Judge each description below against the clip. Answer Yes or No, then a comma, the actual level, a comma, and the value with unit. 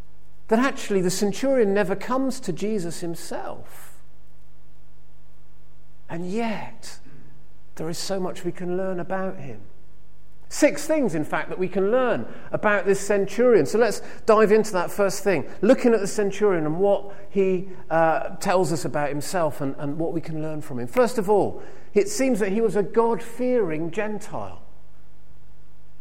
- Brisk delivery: No, average, 160 wpm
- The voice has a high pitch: Yes, high, 195 Hz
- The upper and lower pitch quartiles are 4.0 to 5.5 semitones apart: Yes, average, 4.7 semitones